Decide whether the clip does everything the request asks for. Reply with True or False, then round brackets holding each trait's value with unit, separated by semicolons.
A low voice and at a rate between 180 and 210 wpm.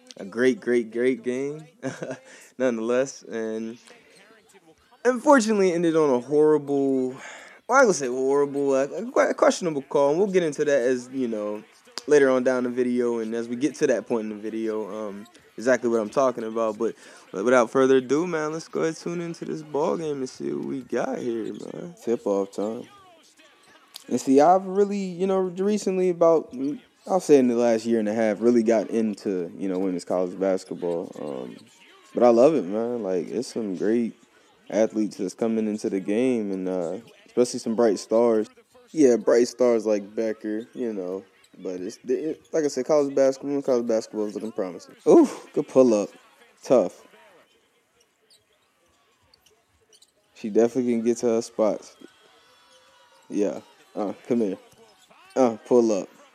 False (125 Hz; 170 wpm)